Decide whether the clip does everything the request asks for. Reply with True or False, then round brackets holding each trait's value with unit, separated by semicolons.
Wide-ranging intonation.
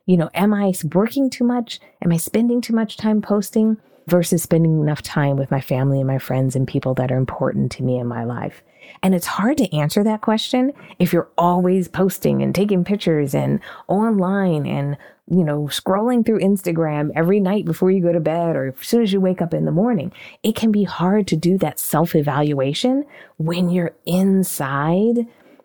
True (6.0 semitones)